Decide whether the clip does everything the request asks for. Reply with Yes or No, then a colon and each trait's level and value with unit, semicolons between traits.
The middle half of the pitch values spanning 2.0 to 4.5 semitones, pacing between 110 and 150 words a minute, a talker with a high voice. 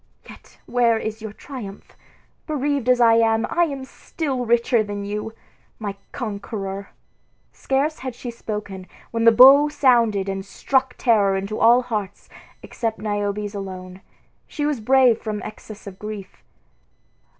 Yes: average, 3.7 semitones; average, 140 wpm; high, 225 Hz